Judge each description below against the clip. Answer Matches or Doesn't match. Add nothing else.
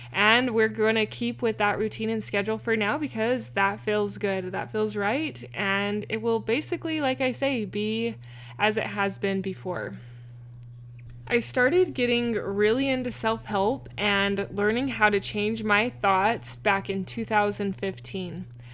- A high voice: Matches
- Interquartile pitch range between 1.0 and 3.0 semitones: Matches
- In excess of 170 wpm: Doesn't match